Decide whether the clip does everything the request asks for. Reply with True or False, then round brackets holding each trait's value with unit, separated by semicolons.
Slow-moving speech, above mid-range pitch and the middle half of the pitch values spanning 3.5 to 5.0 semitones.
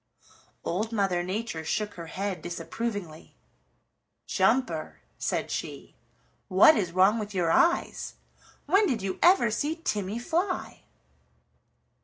True (115 wpm; 210 Hz; 4.5 semitones)